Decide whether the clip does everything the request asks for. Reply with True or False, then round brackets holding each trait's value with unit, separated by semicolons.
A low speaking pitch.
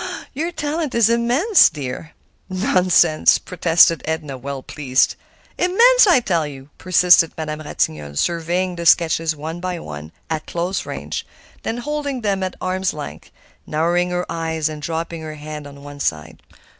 False (165 Hz)